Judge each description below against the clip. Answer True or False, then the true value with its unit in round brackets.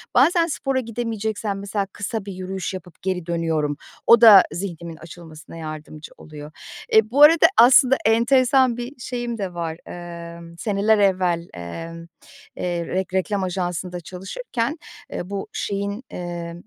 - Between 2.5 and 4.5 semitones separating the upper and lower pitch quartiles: False (5.1 semitones)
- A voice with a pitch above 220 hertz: False (190 Hz)